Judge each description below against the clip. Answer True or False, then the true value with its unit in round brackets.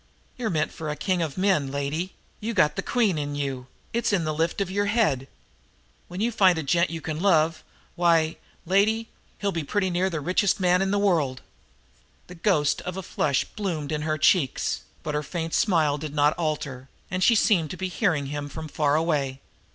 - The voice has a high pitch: False (165 Hz)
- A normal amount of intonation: True (4.2 semitones)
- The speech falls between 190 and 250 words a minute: True (205 wpm)